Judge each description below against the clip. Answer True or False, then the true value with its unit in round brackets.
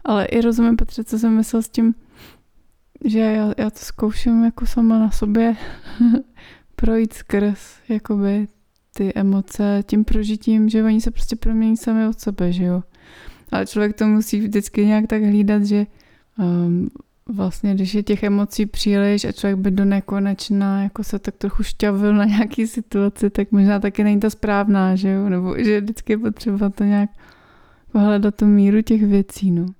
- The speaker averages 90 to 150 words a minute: False (170 wpm)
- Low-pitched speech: False (210 Hz)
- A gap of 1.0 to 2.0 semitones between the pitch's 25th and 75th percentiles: True (1.7 semitones)